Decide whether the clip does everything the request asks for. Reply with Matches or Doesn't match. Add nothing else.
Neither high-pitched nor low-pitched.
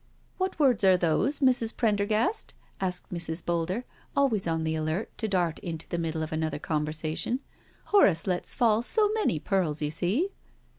Matches